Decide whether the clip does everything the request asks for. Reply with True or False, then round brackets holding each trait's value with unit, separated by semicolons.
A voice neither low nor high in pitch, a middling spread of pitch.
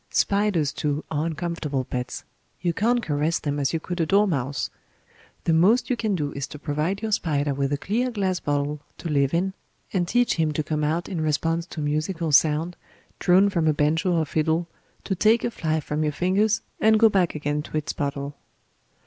True (160 Hz; 4.3 semitones)